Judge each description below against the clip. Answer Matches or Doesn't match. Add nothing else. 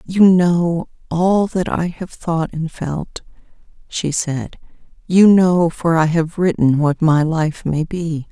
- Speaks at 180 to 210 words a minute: Doesn't match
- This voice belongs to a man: Doesn't match